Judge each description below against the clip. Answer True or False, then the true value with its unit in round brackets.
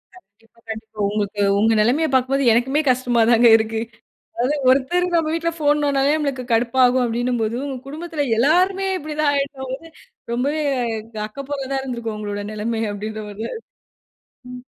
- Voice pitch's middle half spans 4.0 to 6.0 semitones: True (4.4 semitones)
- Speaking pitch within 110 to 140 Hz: False (255 Hz)